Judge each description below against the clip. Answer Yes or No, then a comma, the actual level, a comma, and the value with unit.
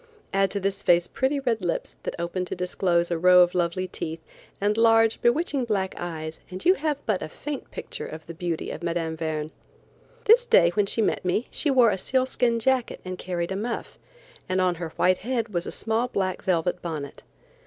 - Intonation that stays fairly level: No, average, 5.1 semitones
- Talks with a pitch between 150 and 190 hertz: Yes, medium, 185 Hz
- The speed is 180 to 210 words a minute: Yes, average, 200 wpm